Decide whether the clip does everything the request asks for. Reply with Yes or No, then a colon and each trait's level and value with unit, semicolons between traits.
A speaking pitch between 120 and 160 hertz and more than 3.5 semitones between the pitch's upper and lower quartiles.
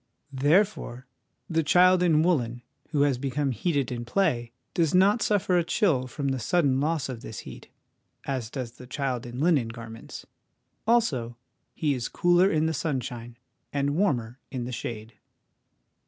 Yes: medium, 140 Hz; wide, 5.6 semitones